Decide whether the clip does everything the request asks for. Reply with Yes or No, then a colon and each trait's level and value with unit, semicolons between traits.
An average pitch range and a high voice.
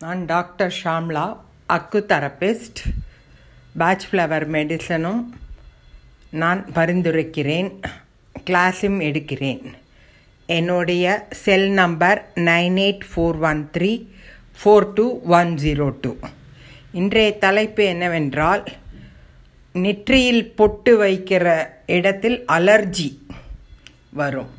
No: average, 4.5 semitones; medium, 175 Hz